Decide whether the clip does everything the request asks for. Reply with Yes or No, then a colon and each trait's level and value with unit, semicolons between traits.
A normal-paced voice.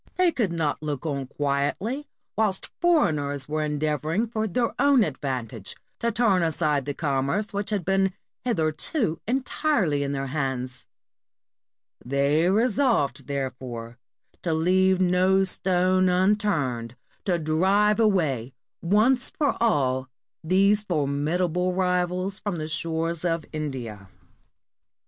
No: slow, 120 wpm